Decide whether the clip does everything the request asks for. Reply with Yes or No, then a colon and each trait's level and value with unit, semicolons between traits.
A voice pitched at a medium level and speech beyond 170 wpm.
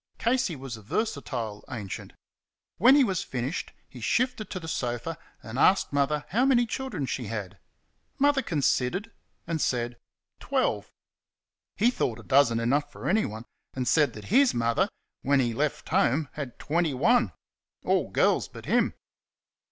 No: medium, 145 Hz; average, 150 wpm